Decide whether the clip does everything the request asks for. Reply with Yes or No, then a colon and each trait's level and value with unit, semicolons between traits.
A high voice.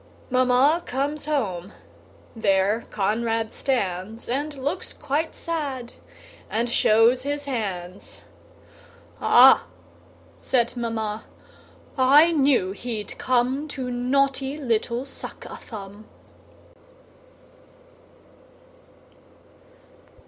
Yes: high, 245 Hz